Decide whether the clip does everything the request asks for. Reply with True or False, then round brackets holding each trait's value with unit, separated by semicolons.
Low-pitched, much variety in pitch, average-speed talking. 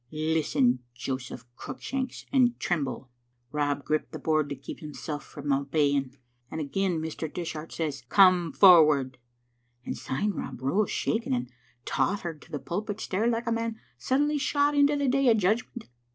False (165 Hz; 7.8 semitones; 165 wpm)